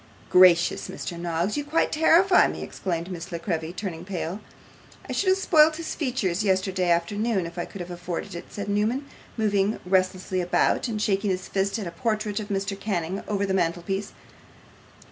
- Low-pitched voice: No, high, 195 Hz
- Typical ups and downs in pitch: Yes, average, 3.4 semitones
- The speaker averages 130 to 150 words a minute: No, average, 180 wpm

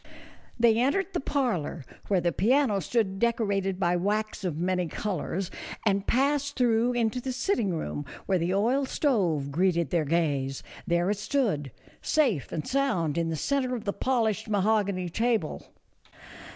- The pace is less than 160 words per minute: Yes, average, 150 wpm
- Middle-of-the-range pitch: No, high, 200 Hz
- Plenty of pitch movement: Yes, wide, 5.9 semitones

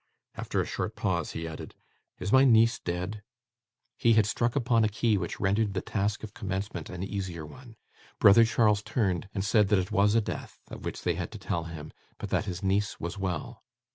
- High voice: No, low, 100 Hz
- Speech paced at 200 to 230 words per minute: Yes, fast, 205 wpm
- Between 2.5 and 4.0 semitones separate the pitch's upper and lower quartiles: Yes, average, 3.2 semitones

